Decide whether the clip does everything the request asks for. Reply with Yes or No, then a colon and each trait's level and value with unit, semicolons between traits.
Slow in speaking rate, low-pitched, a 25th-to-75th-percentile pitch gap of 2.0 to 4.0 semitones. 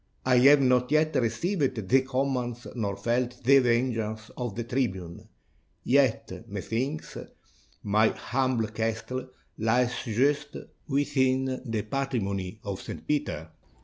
Yes: slow, 120 wpm; low, 125 Hz; average, 3.2 semitones